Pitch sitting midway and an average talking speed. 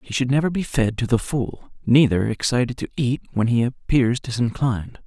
No: low, 125 Hz; average, 190 wpm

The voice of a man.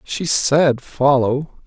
Yes: male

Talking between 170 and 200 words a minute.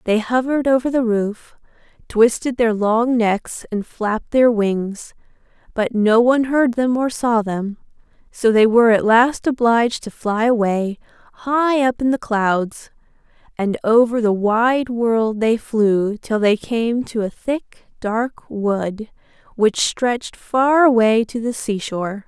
No: average, 155 wpm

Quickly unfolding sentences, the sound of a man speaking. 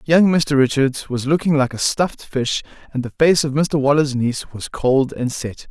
Yes: fast, 210 wpm; male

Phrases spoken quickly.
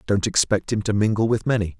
Yes: fast, 235 wpm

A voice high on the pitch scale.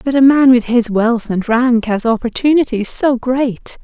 Yes: high, 245 Hz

